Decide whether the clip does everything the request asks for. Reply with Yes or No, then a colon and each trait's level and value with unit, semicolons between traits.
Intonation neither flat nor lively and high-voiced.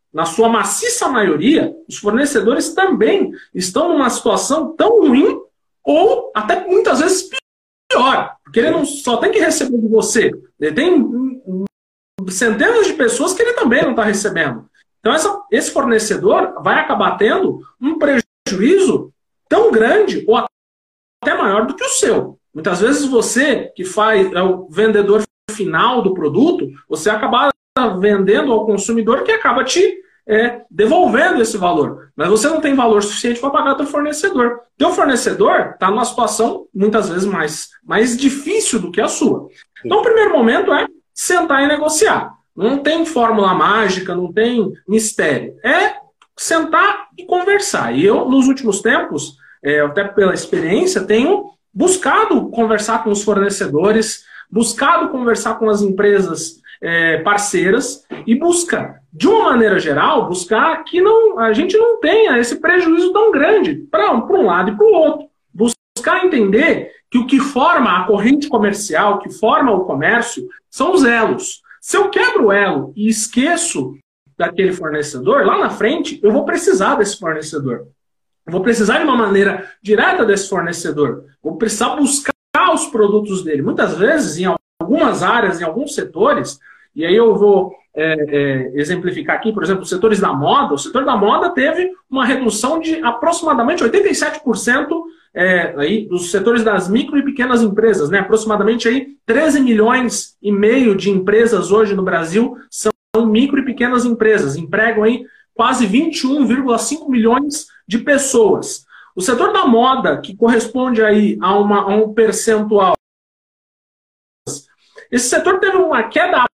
No: wide, 7.3 semitones; high, 235 Hz